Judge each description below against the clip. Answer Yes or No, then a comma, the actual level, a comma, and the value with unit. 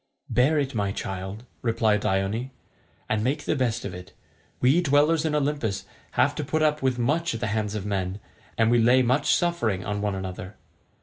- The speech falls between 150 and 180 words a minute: No, average, 190 wpm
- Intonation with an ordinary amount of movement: No, wide, 5.9 semitones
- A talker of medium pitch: No, low, 115 Hz